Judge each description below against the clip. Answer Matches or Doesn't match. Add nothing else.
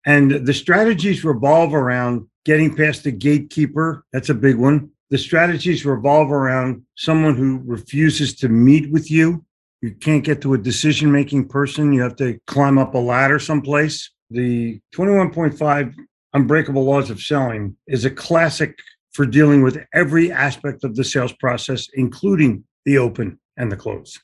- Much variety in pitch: Doesn't match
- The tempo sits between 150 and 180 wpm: Matches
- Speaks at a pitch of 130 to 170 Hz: Matches